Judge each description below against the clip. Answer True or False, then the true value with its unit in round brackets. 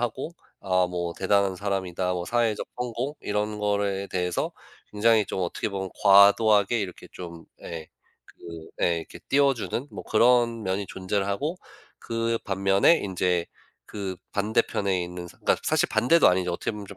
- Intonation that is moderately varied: True (3.6 semitones)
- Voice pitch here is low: True (100 Hz)